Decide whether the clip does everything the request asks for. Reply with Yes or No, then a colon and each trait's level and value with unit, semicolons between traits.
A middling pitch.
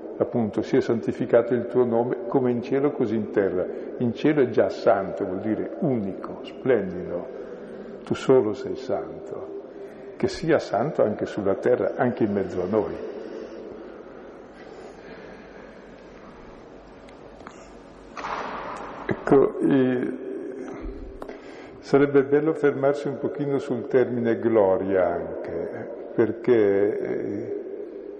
Yes: medium, 145 Hz